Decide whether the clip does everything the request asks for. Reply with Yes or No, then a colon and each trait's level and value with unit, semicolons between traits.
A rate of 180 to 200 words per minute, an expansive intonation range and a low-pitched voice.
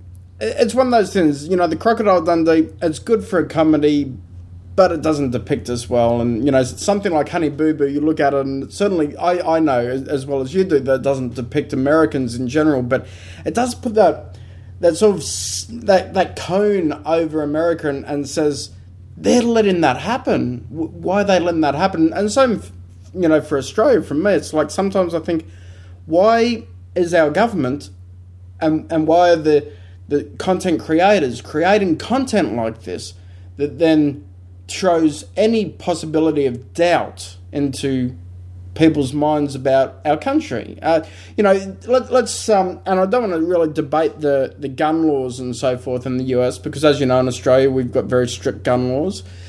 No: average, 185 wpm; wide, 6.1 semitones; medium, 145 Hz